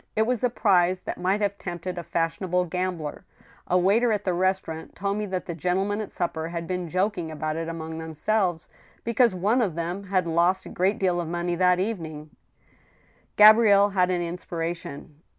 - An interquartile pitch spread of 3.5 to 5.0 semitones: No, average, 2.9 semitones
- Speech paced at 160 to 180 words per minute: No, average, 195 wpm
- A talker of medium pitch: Yes, medium, 180 Hz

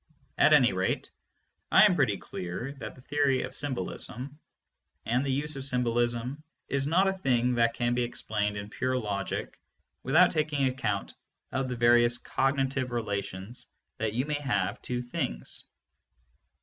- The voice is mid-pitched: No, low, 125 Hz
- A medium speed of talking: Yes, average, 155 wpm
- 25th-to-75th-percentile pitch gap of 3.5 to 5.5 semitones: No, average, 3.0 semitones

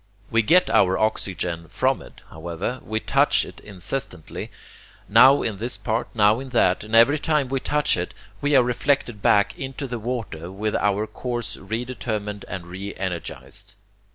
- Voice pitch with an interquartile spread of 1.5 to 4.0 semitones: No, average, 4.5 semitones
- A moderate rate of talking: Yes, average, 165 wpm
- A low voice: Yes, low, 110 Hz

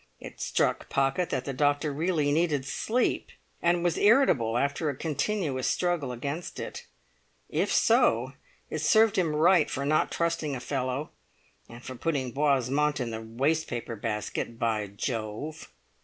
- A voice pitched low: No, medium, 145 Hz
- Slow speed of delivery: No, average, 145 wpm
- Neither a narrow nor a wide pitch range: Yes, average, 4.3 semitones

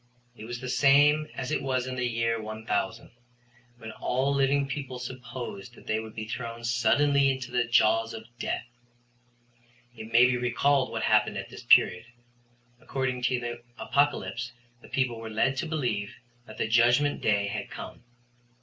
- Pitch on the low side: Yes, low, 125 Hz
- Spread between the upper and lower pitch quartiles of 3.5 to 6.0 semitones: No, average, 2.9 semitones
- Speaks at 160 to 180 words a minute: Yes, average, 165 wpm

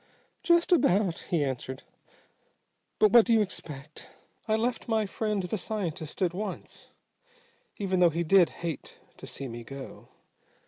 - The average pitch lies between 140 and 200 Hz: Yes, medium, 185 Hz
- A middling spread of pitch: No, wide, 5.7 semitones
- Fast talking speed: No, average, 145 wpm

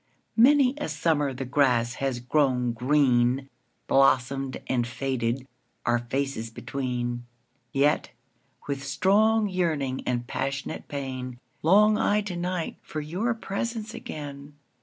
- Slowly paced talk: Yes, slow, 105 wpm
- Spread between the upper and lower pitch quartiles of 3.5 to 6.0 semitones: Yes, average, 5.3 semitones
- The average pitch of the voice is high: No, low, 135 Hz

